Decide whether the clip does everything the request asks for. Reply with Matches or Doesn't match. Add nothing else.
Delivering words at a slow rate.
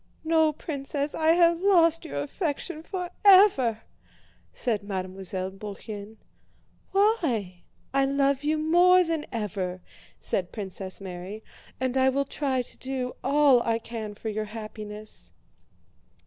Matches